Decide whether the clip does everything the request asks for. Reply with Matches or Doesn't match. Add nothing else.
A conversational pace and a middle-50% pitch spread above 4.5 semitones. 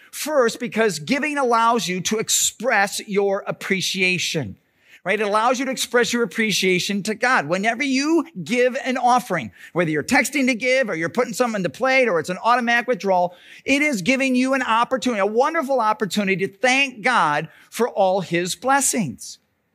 Matches